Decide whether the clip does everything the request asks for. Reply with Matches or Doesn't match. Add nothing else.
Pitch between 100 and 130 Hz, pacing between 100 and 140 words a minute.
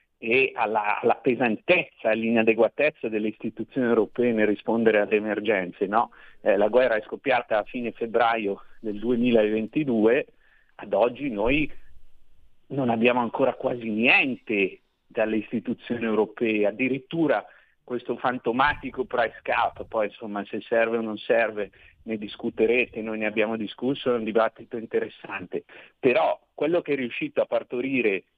Matches